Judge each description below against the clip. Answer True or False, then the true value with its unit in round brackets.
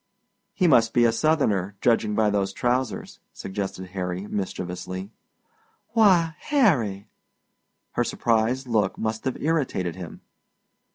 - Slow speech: True (110 wpm)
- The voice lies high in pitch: False (110 Hz)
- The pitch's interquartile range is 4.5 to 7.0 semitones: True (5.4 semitones)